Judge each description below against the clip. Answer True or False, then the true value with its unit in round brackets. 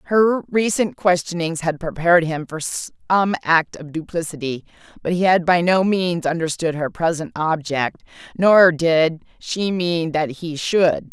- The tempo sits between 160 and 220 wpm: False (150 wpm)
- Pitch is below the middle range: False (170 Hz)